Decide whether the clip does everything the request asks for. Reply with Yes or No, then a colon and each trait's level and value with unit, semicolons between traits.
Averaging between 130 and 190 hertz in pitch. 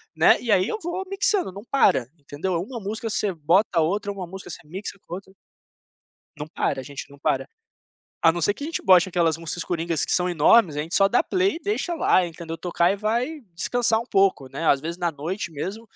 Yes: medium, 185 Hz